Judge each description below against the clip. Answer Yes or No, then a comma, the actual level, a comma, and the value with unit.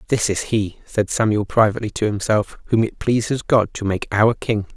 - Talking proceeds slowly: No, average, 200 wpm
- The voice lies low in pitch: Yes, low, 105 Hz